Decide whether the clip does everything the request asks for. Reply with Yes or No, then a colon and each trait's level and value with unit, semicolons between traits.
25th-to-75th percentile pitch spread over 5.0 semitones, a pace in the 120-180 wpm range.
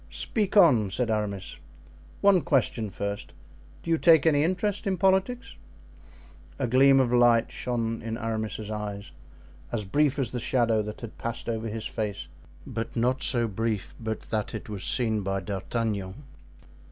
No: average, 4.1 semitones; average, 155 wpm